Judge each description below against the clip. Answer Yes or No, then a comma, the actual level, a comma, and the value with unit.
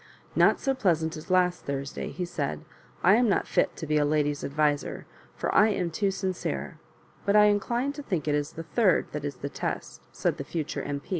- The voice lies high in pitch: No, medium, 165 Hz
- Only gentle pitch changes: No, wide, 5.4 semitones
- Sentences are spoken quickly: Yes, fast, 215 wpm